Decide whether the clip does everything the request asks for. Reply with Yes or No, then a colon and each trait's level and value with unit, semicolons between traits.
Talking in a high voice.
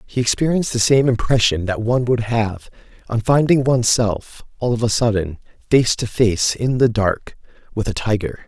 No: low, 115 Hz